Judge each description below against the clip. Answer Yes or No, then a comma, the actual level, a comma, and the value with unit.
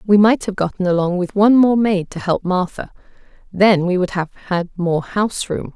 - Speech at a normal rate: No, fast, 210 wpm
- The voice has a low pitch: No, high, 190 Hz